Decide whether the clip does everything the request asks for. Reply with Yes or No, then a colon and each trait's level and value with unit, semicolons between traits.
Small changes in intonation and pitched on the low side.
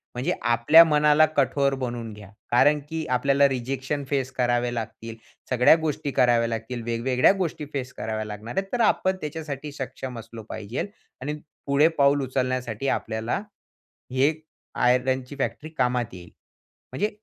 No: average, 3.6 semitones; low, 130 Hz